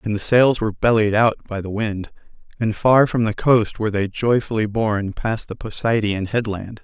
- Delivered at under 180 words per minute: No, average, 195 wpm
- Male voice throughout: Yes, male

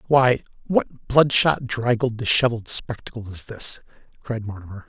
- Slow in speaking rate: Yes, slow, 125 wpm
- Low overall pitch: Yes, low, 115 Hz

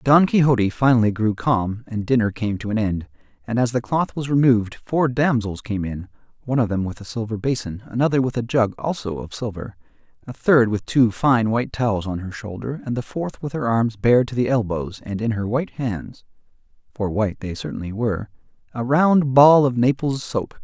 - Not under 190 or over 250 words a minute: Yes, fast, 205 wpm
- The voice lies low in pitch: Yes, low, 115 Hz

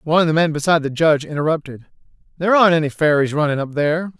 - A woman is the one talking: No, male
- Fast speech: Yes, fast, 215 wpm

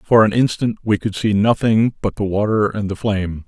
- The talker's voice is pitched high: No, low, 105 Hz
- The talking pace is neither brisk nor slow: No, fast, 225 wpm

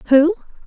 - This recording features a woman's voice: Yes, female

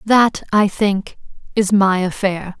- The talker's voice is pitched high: Yes, high, 200 Hz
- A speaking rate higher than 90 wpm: Yes, average, 140 wpm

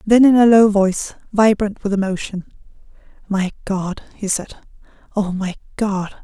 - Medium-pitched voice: No, high, 200 Hz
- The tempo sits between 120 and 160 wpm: Yes, average, 145 wpm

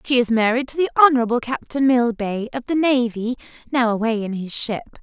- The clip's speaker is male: No, female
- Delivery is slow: No, average, 190 wpm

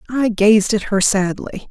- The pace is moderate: Yes, average, 175 wpm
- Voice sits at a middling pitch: No, high, 210 Hz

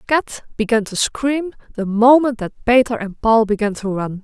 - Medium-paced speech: Yes, average, 185 wpm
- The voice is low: No, high, 230 Hz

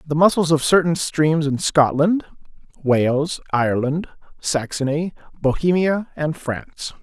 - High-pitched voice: No, medium, 155 Hz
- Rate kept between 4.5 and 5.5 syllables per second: No, 4.3 syllables/s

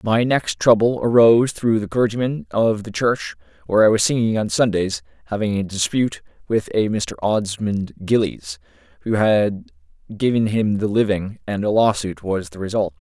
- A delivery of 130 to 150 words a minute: No, average, 165 wpm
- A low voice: Yes, low, 105 Hz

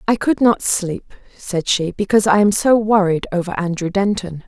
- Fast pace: No, average, 190 wpm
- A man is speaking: No, female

